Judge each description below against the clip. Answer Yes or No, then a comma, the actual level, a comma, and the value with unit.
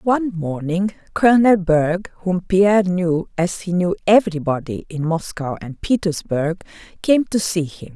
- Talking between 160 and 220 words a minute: No, average, 145 wpm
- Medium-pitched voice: Yes, medium, 180 Hz